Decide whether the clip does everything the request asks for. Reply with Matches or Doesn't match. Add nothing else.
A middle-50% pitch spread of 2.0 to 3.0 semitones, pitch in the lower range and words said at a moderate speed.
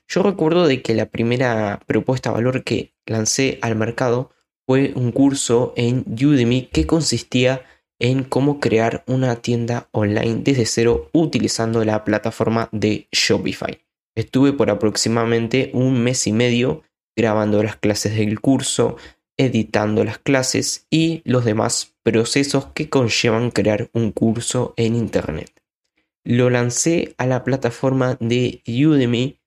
Matches